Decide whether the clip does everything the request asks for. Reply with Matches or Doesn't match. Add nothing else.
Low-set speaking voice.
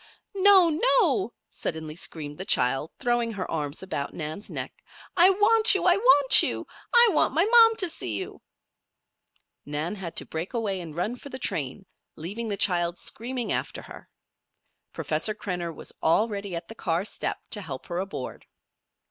Doesn't match